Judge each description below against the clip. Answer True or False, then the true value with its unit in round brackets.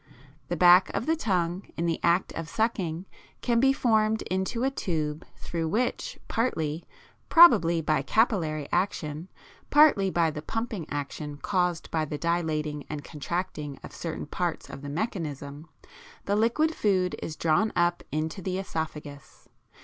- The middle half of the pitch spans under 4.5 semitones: False (5.2 semitones)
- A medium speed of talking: True (150 wpm)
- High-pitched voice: False (170 Hz)